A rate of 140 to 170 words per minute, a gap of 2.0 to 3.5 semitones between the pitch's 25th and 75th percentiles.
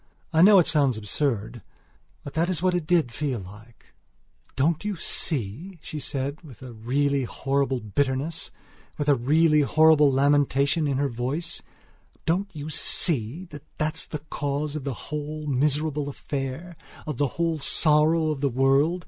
Yes: average, 155 wpm; average, 2.9 semitones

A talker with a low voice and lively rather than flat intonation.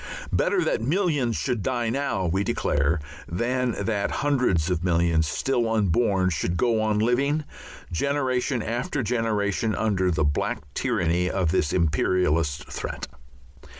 Yes: low, 105 Hz; wide, 6.2 semitones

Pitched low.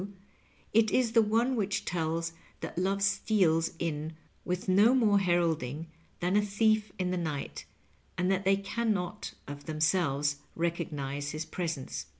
No: medium, 180 Hz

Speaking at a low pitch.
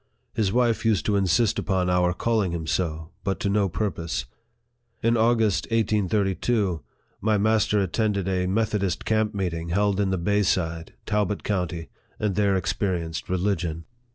Yes: low, 100 Hz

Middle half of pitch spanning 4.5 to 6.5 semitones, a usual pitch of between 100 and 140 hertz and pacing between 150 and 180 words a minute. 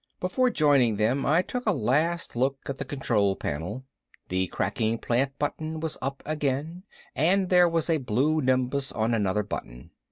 Yes: wide, 5.6 semitones; low, 135 Hz; average, 165 wpm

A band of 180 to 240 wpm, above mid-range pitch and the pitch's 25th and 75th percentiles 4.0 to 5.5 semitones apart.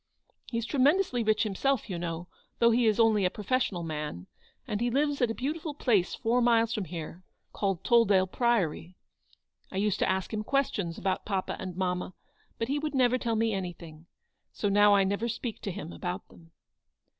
Yes: average, 190 wpm; high, 210 Hz; average, 4.5 semitones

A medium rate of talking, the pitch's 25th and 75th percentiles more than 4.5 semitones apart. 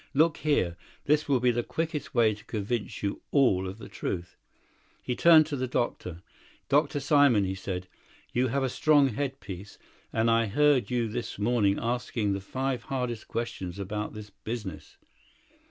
Yes: average, 170 wpm; average, 5.0 semitones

